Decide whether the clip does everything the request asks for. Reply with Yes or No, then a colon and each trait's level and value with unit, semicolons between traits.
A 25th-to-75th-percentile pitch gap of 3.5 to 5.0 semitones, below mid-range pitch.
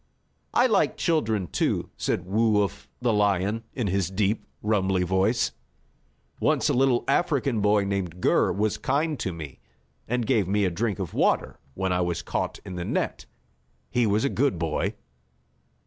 Yes: average, 4.1 semitones; low, 105 Hz